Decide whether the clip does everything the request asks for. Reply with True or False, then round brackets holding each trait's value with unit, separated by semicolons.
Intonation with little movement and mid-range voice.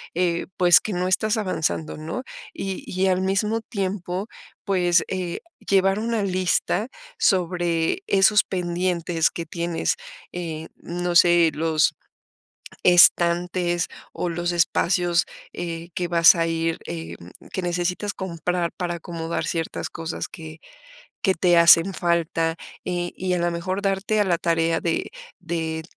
True (1.9 semitones; 175 Hz)